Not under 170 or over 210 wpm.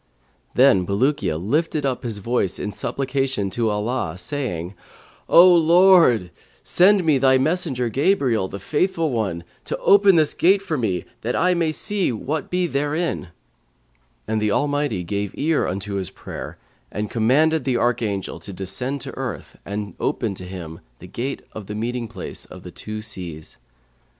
No: average, 160 wpm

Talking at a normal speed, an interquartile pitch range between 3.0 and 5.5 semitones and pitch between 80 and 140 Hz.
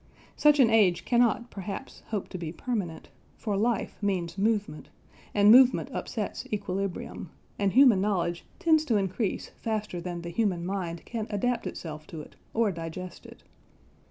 No: average, 155 wpm; average, 4.5 semitones; high, 200 Hz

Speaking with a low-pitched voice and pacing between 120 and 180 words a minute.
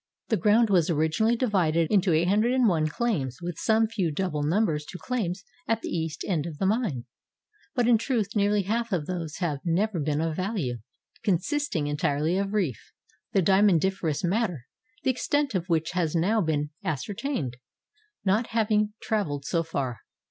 No: medium, 185 Hz; average, 165 wpm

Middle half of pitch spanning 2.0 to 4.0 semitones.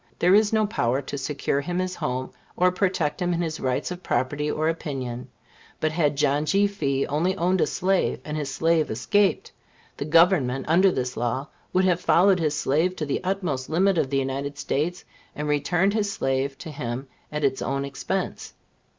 No: average, 4.9 semitones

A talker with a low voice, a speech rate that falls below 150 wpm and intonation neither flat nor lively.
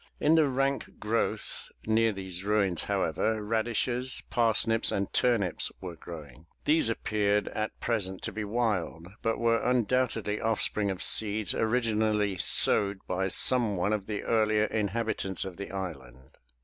Yes: low, 105 Hz; average, 140 wpm; average, 3.0 semitones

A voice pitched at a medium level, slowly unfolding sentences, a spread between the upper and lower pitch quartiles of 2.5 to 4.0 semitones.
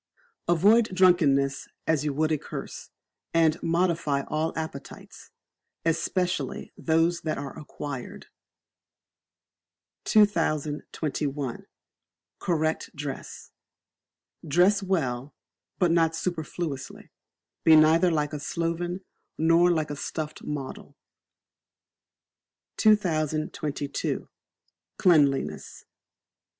Yes: medium, 160 Hz; slow, 80 wpm; average, 2.8 semitones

